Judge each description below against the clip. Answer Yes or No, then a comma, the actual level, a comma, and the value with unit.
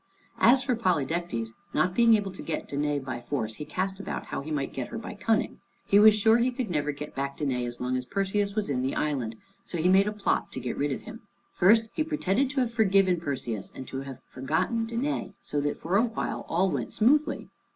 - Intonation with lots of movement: Yes, wide, 8.1 semitones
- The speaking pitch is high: No, medium, 180 Hz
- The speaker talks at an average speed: No, fast, 230 wpm